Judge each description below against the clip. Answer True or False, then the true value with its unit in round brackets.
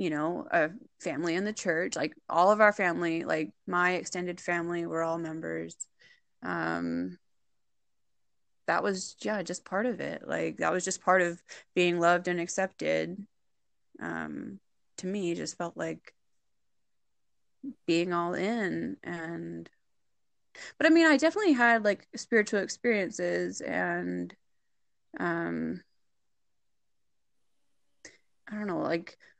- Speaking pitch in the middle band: True (175 Hz)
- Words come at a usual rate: False (130 wpm)